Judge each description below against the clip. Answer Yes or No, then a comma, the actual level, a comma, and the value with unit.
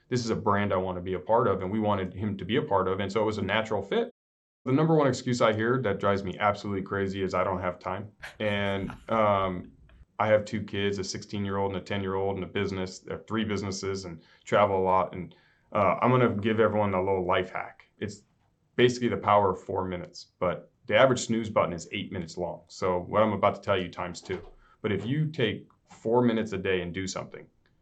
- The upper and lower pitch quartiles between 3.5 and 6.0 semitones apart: No, average, 2.8 semitones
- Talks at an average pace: No, fast, 250 wpm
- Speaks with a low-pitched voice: Yes, low, 100 Hz